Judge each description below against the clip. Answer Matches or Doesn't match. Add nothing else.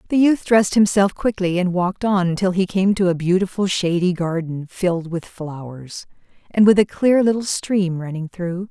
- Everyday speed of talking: Matches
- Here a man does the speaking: Doesn't match